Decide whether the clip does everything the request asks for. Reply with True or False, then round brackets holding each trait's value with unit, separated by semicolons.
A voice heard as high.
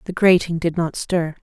False (170 Hz)